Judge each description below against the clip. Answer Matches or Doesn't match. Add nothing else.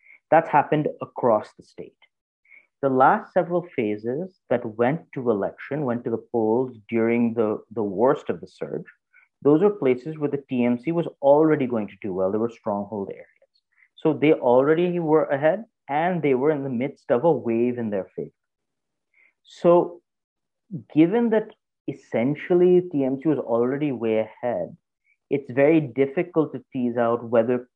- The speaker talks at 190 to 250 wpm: Doesn't match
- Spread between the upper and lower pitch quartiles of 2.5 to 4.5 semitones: Doesn't match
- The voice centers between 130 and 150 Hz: Matches